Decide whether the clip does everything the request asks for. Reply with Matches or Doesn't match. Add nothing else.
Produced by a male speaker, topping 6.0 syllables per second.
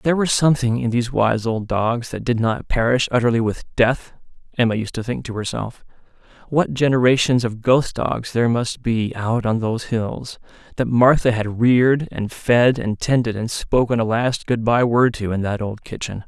Doesn't match